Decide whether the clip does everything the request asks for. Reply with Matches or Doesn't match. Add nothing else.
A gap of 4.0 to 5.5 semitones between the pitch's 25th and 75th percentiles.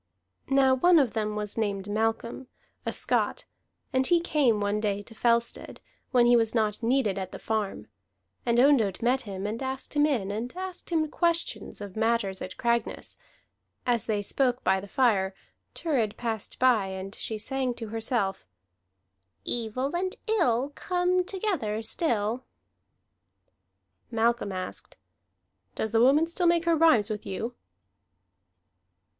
Matches